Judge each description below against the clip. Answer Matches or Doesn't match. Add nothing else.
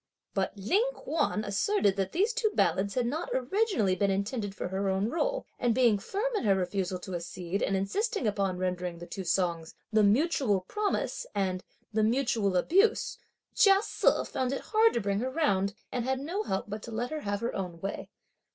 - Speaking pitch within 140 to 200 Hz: Doesn't match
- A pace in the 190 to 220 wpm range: Matches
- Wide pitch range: Matches